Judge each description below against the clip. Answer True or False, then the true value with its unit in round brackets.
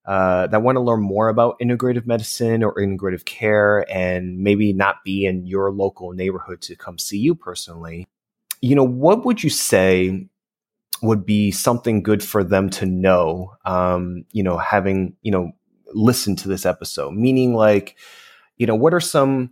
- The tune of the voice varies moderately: True (4.2 semitones)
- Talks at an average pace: True (170 wpm)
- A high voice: False (100 Hz)